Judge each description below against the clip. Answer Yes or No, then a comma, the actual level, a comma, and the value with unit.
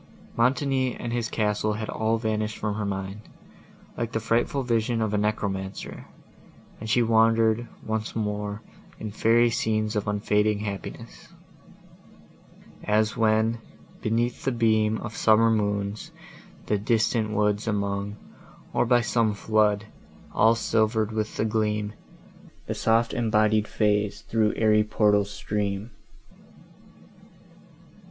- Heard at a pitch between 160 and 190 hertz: No, low, 110 Hz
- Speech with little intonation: Yes, narrow, 1.4 semitones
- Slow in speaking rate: Yes, slow, 120 wpm